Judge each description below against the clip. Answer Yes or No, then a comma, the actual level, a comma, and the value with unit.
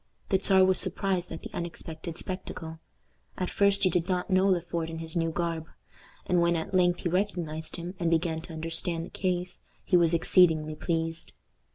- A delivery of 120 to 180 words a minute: No, average, 190 wpm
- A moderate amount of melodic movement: No, narrow, 2.0 semitones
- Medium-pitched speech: Yes, medium, 170 Hz